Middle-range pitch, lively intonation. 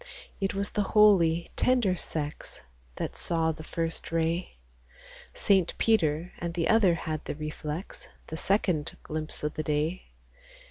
No: medium, 165 Hz; average, 3.7 semitones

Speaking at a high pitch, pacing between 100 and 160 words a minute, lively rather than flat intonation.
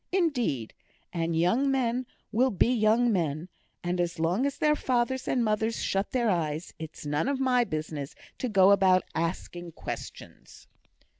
Yes: high, 200 Hz; average, 155 wpm; wide, 6.9 semitones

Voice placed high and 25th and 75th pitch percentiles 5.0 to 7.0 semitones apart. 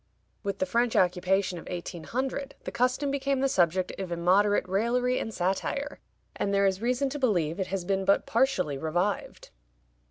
Yes: high, 200 Hz; wide, 5.5 semitones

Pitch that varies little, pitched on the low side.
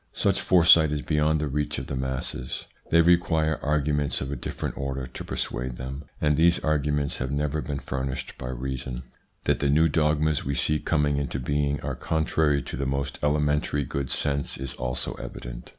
Yes: narrow, 2.2 semitones; very low, 70 Hz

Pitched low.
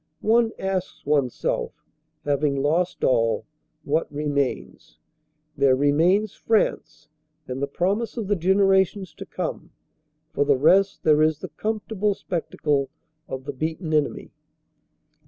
No: medium, 155 Hz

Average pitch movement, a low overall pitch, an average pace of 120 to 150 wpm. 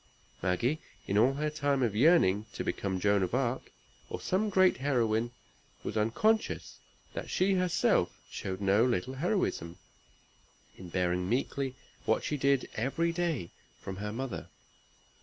No: wide, 7.1 semitones; low, 125 Hz; average, 140 wpm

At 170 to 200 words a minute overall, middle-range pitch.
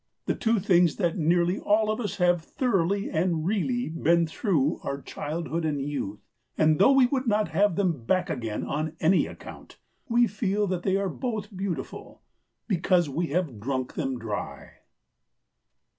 No: average, 160 wpm; medium, 175 Hz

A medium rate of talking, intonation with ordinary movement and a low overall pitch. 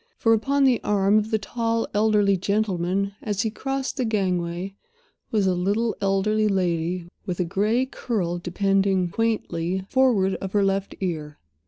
No: average, 155 wpm; average, 3.2 semitones; high, 200 Hz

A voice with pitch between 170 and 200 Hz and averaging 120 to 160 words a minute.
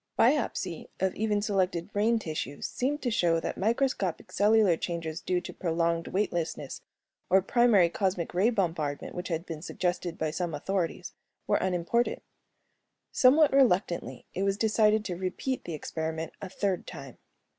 Yes: medium, 185 Hz; average, 145 wpm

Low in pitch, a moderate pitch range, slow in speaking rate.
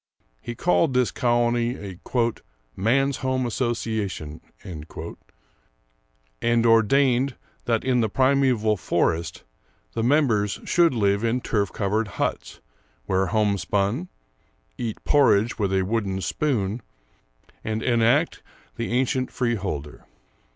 Yes: low, 115 Hz; average, 4.1 semitones; slow, 105 wpm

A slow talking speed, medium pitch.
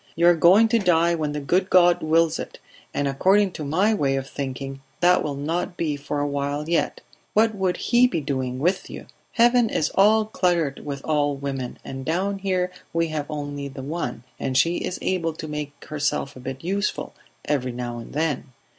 No: average, 200 wpm; medium, 155 Hz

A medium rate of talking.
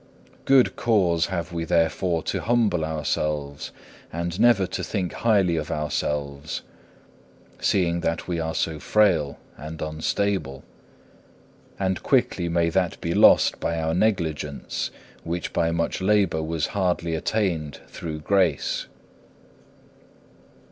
No: slow, 120 wpm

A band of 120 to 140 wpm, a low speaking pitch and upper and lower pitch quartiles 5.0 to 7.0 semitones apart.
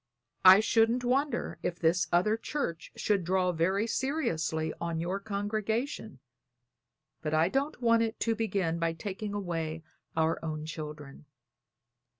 No: slow, 135 wpm; medium, 185 Hz; wide, 5.4 semitones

